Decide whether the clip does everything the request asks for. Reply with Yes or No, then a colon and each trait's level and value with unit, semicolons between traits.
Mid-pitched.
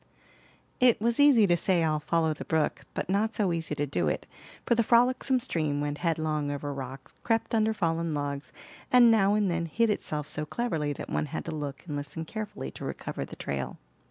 Yes: medium, 165 Hz